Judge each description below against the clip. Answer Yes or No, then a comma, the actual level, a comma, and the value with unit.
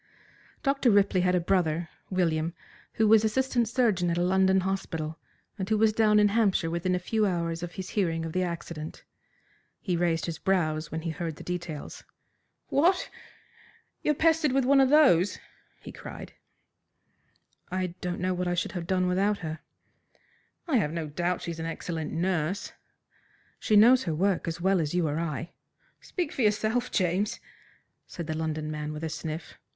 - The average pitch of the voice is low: No, medium, 180 Hz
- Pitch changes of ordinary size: Yes, average, 4.2 semitones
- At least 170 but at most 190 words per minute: Yes, average, 175 wpm